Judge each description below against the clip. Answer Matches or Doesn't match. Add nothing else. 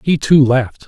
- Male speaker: Matches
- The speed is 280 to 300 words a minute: Doesn't match